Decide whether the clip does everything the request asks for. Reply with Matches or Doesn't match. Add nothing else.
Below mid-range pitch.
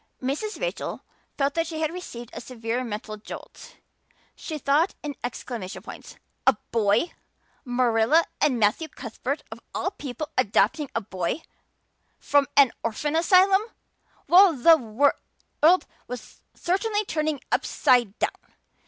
Doesn't match